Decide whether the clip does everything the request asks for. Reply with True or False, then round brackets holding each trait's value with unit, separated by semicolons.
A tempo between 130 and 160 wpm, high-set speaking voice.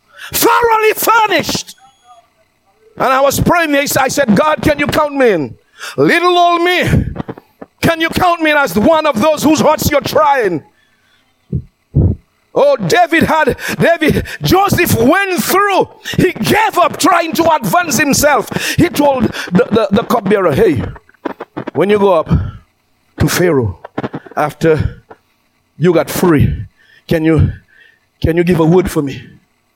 True (140 wpm; 280 Hz)